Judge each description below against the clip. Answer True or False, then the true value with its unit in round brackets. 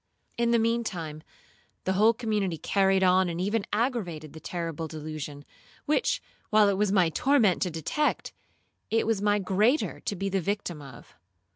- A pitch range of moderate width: True (4.8 semitones)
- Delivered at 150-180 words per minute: True (165 wpm)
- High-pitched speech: True (195 Hz)